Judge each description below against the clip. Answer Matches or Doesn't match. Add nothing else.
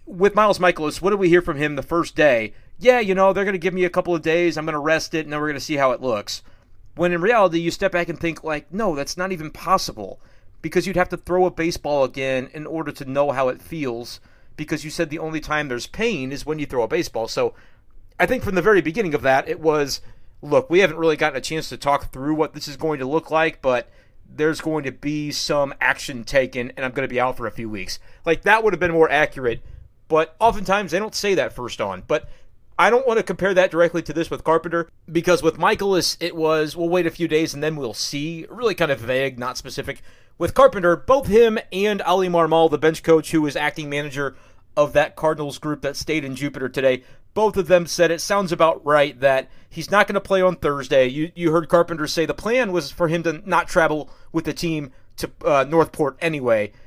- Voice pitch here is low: Doesn't match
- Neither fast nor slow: Doesn't match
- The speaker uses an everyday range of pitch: Matches